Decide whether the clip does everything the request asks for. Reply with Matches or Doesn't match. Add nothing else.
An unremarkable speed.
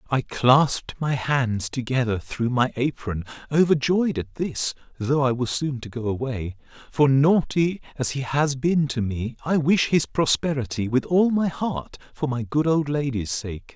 Matches